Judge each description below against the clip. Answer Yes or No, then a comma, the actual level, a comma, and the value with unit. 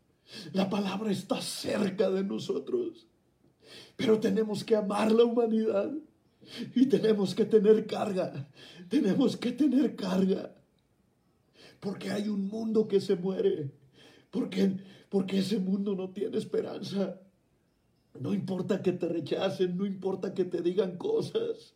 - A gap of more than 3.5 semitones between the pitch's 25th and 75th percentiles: No, average, 2.9 semitones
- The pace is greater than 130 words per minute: No, slow, 125 wpm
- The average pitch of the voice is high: Yes, high, 200 Hz